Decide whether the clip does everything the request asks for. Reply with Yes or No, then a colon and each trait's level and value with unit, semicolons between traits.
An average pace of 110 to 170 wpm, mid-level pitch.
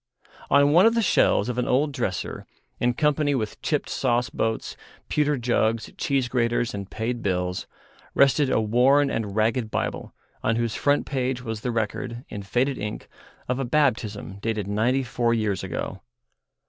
No: average, 165 wpm; low, 120 Hz